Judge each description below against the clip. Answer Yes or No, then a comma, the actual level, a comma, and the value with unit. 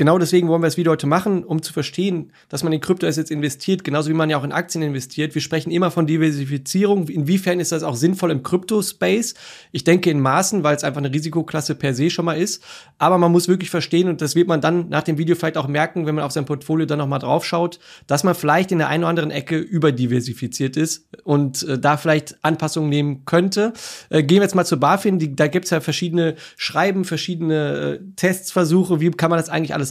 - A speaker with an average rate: No, fast, 230 wpm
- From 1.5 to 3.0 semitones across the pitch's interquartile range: Yes, average, 2.7 semitones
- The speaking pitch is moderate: Yes, medium, 160 Hz